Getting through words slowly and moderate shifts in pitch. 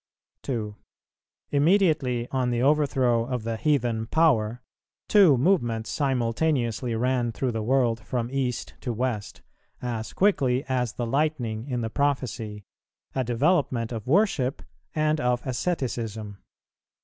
Yes: slow, 125 wpm; average, 3.5 semitones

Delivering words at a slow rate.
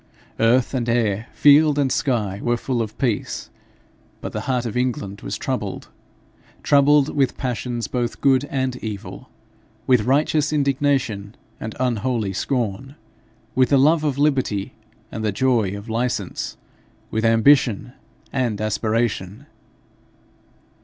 Yes: slow, 125 wpm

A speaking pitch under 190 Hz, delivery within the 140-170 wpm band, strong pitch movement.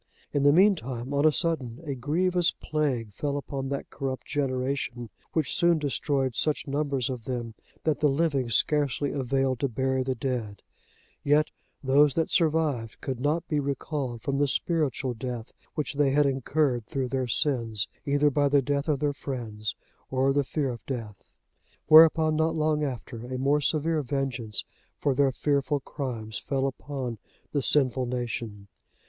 No: low, 135 Hz; average, 160 wpm; average, 2.8 semitones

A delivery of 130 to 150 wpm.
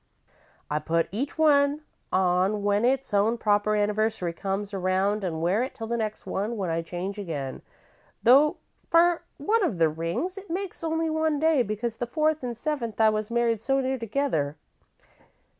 No: average, 175 wpm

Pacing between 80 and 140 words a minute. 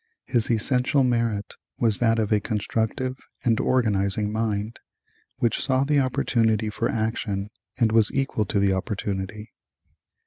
Yes: slow, 135 wpm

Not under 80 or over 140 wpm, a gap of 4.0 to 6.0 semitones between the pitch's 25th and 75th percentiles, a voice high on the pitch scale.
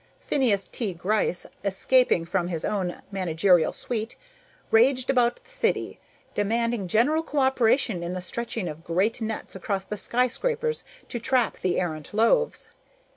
Yes: slow, 135 wpm; wide, 5.5 semitones; high, 220 Hz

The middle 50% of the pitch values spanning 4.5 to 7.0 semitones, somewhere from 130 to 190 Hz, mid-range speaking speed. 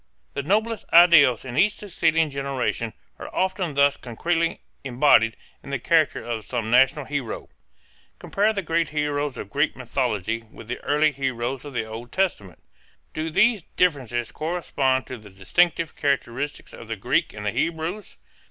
Yes: wide, 5.6 semitones; medium, 140 Hz; average, 155 wpm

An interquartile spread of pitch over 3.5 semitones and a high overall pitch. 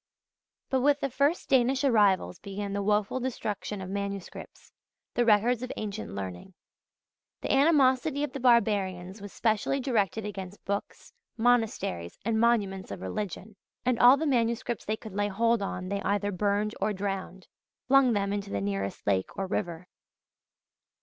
Yes: average, 4.0 semitones; high, 210 Hz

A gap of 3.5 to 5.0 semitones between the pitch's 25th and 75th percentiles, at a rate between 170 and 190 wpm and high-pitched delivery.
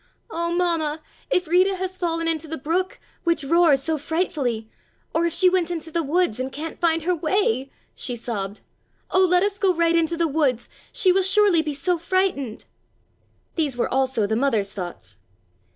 Yes: average, 4.7 semitones; average, 180 wpm; very high, 325 Hz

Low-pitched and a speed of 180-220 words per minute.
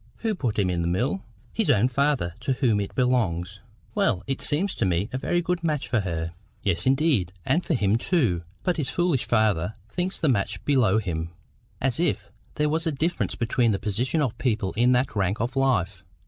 Yes: low, 120 Hz; fast, 205 wpm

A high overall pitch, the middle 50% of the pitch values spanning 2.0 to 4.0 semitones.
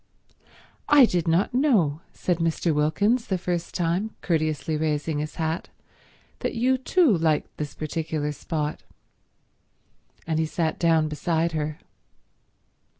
No: medium, 165 Hz; average, 2.7 semitones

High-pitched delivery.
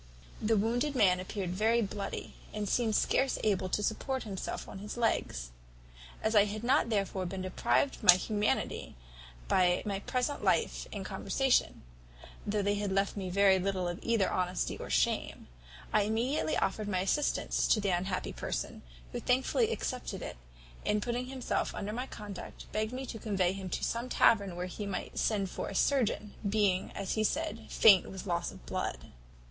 Yes: high, 205 Hz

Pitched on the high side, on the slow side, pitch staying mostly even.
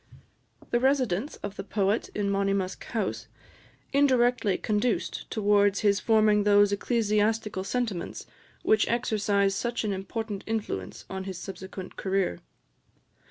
Yes: high, 205 Hz; slow, 115 wpm; narrow, 2.3 semitones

